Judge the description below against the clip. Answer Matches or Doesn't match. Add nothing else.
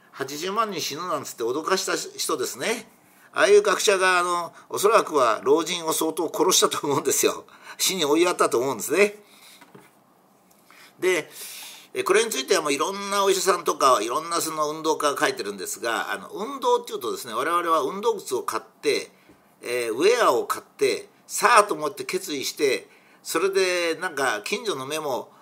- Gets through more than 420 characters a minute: Doesn't match